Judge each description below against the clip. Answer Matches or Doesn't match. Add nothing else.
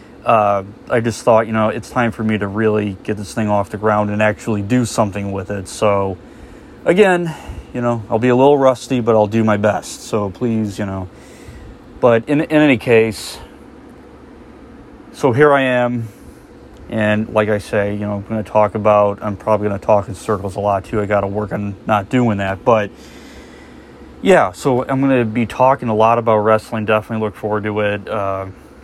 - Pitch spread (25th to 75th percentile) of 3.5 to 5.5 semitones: Doesn't match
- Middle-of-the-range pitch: Doesn't match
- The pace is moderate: Matches